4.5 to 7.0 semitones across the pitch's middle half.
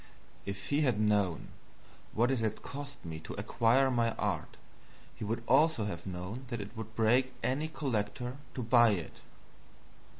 No: average, 3.9 semitones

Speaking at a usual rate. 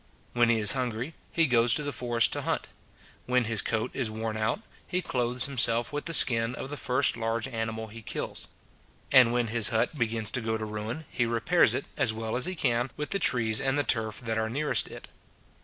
No: fast, 220 wpm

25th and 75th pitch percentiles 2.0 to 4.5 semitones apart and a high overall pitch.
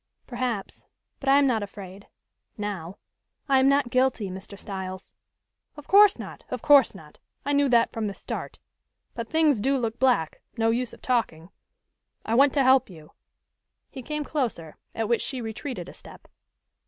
No: average, 5.2 semitones; high, 235 Hz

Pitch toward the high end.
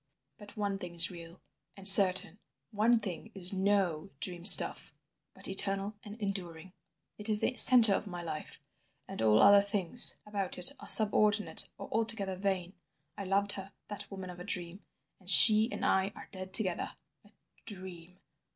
Yes: high, 195 Hz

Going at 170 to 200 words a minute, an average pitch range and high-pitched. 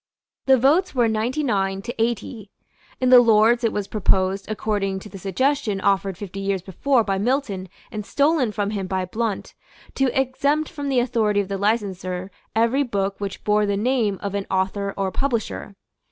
Yes: average, 180 wpm; average, 4.0 semitones; high, 210 Hz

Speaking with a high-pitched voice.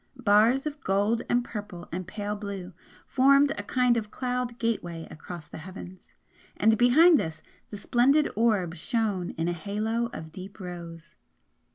Yes: high, 210 Hz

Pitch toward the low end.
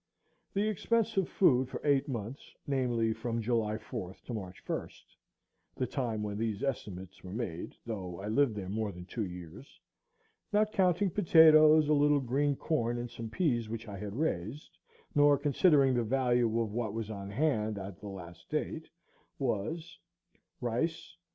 Yes: low, 120 Hz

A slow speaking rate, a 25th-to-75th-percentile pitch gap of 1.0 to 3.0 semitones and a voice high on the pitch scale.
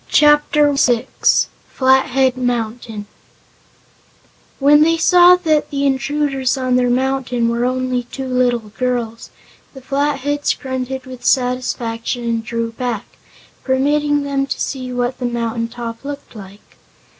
Yes: slow, 125 wpm; narrow, 2.6 semitones; very high, 255 Hz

